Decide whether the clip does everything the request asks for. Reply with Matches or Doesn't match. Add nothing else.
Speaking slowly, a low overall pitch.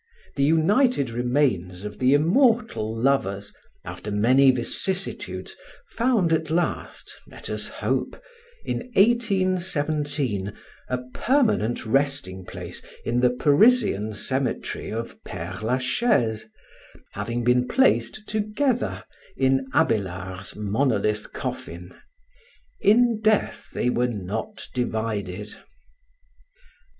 Matches